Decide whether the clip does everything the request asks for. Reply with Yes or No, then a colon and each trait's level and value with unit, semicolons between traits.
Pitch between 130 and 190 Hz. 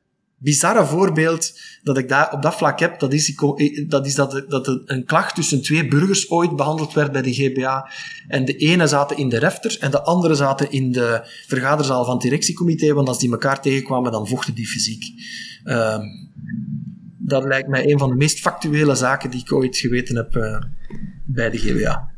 Yes: medium, 140 Hz